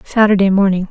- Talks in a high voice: Yes, high, 195 Hz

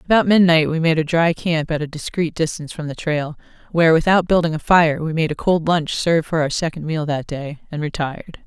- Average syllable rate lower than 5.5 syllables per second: No, 5.7 syllables/s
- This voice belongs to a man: No, female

